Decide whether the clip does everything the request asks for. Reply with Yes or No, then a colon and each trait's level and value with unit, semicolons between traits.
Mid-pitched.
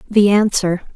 No: high, 200 Hz